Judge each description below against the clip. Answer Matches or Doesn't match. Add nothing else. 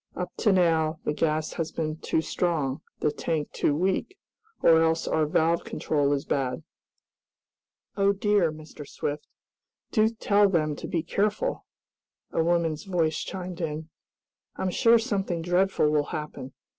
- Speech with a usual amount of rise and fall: Matches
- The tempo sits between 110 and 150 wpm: Matches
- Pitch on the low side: Doesn't match